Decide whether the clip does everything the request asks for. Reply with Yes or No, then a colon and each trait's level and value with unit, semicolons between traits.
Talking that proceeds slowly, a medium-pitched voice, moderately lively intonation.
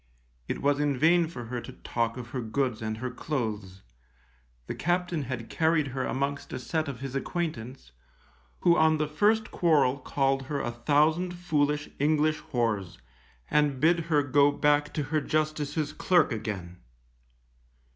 No: average, 155 wpm; medium, 145 Hz; average, 3.8 semitones